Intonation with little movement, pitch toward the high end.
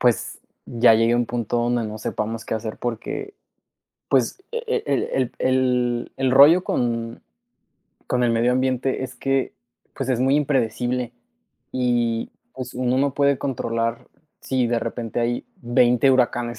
No: narrow, 2.0 semitones; low, 125 Hz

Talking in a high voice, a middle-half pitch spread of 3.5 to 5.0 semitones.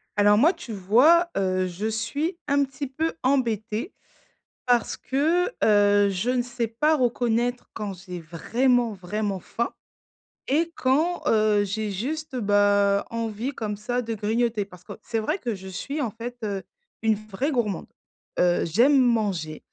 Yes: high, 225 Hz; average, 4.2 semitones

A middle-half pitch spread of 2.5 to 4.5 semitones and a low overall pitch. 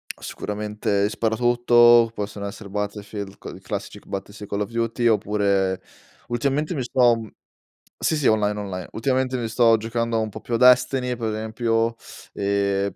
Yes: average, 2.8 semitones; low, 110 Hz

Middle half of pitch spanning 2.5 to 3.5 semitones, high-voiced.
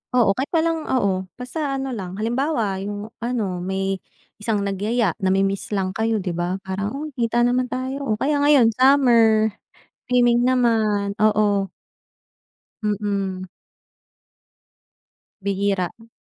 No: average, 4.2 semitones; high, 215 Hz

